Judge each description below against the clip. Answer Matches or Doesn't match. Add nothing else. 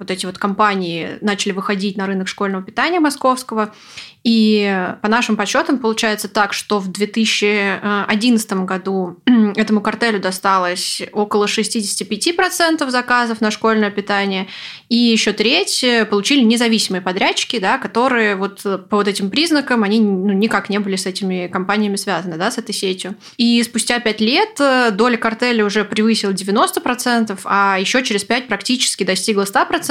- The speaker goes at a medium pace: Matches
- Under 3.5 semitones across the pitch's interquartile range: Matches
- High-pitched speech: Matches